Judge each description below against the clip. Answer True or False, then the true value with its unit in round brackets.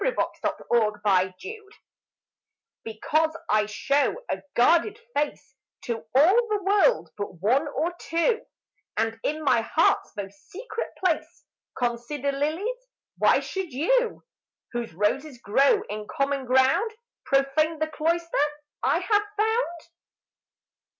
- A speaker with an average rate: False (120 wpm)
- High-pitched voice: True (295 Hz)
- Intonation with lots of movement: True (7.1 semitones)